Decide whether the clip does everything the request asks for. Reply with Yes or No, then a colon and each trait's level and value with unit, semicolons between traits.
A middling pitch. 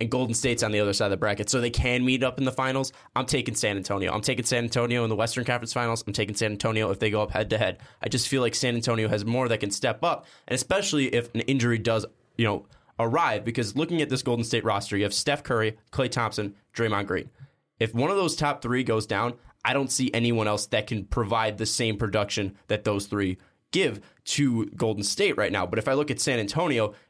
No: low, 115 Hz